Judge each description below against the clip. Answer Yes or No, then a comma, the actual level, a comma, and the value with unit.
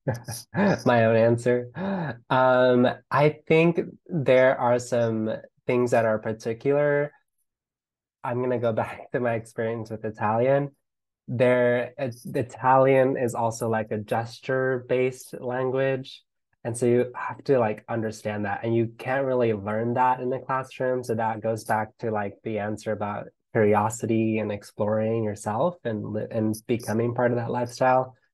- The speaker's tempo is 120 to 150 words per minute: Yes, average, 145 wpm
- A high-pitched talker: No, low, 120 Hz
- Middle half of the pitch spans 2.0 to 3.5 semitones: Yes, narrow, 2.6 semitones